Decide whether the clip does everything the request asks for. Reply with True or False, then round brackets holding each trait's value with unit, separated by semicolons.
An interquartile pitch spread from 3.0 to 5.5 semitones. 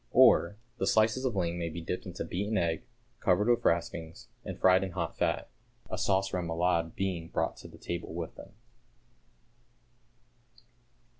False (2.5 semitones)